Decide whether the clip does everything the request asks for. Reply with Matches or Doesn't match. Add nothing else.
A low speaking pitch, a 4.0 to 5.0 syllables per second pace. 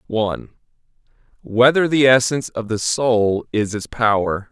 Matches